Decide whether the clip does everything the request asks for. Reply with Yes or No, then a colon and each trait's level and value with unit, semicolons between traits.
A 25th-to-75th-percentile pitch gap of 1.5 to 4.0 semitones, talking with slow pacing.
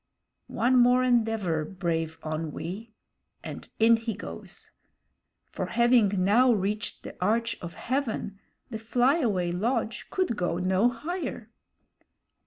No: average, 4.8 semitones; slow, 115 wpm